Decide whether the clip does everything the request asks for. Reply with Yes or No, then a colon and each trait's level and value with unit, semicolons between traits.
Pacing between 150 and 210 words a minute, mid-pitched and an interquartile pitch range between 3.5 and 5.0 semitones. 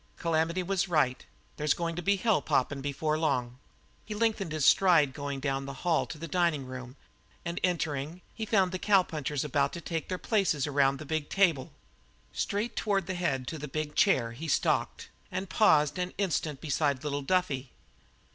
Yes: average, 185 wpm; medium, 155 Hz; average, 4.5 semitones